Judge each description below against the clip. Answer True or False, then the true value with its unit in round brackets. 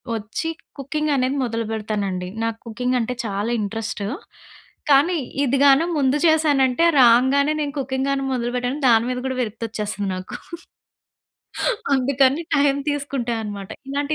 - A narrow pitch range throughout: False (3.8 semitones)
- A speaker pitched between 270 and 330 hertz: False (255 Hz)